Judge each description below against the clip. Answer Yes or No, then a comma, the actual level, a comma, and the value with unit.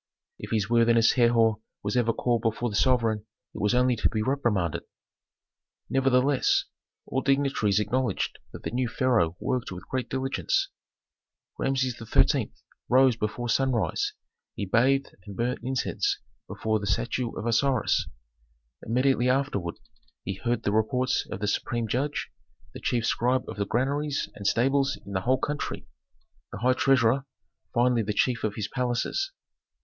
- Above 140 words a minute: Yes, average, 150 wpm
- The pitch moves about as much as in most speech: Yes, average, 3.2 semitones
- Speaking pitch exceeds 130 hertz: No, low, 120 Hz